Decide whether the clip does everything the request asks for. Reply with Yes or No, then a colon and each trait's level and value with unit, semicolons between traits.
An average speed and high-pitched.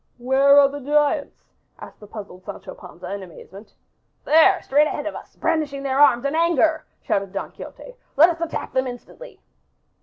Yes: average, 175 wpm; very high, 280 Hz